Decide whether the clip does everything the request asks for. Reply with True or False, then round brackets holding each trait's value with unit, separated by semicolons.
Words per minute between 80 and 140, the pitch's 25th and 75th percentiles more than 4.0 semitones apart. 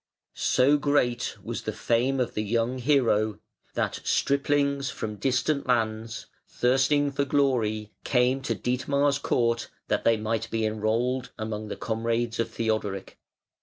False (135 wpm; 3.5 semitones)